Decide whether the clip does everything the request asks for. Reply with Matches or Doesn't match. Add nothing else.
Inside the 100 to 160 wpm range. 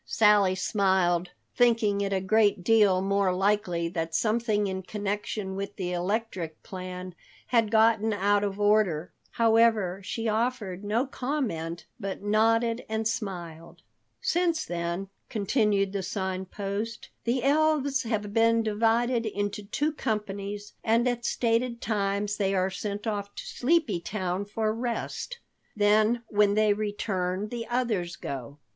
Matches